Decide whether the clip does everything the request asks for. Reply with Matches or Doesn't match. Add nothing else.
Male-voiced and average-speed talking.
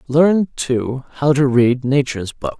Matches